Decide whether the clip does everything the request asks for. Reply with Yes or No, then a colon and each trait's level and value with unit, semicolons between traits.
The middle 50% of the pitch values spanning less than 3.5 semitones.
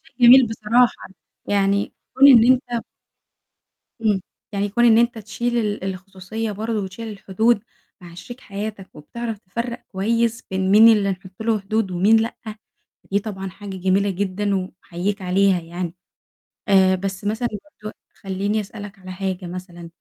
Yes: average, 2.9 semitones